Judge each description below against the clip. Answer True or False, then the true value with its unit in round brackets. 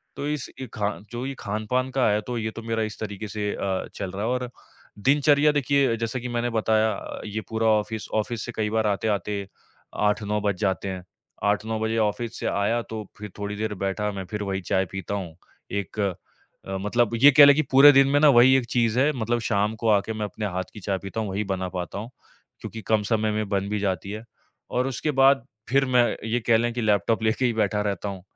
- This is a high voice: False (110 Hz)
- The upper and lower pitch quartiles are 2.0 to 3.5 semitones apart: True (2.8 semitones)